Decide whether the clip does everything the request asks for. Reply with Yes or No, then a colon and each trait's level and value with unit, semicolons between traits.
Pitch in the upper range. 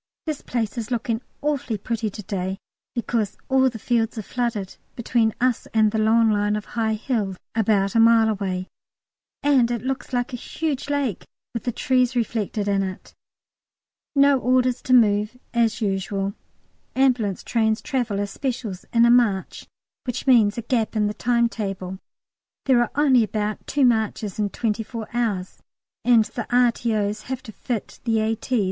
Yes: high, 230 Hz